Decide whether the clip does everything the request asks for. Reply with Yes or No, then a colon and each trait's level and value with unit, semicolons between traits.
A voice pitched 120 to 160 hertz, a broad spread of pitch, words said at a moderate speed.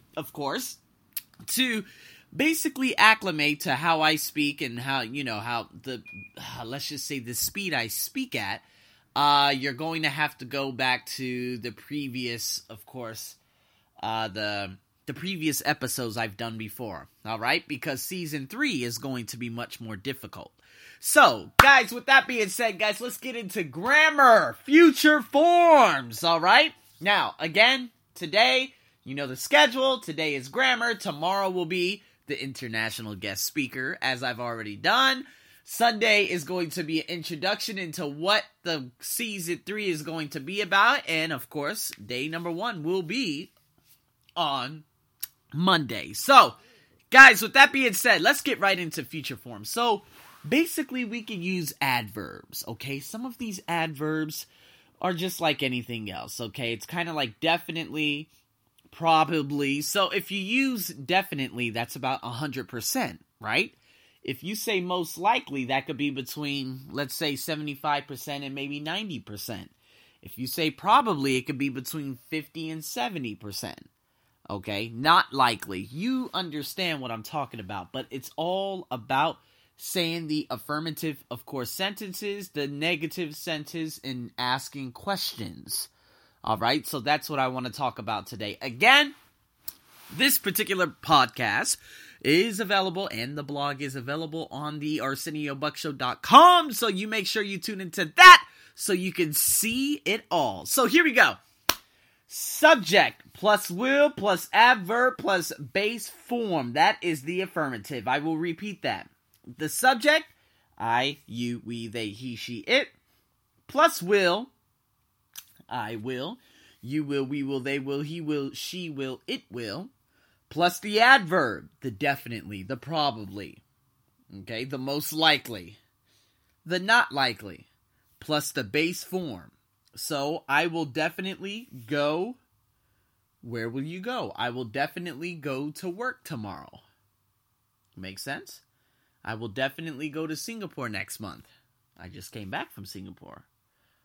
Yes: medium, 150 Hz; wide, 7.2 semitones; average, 145 wpm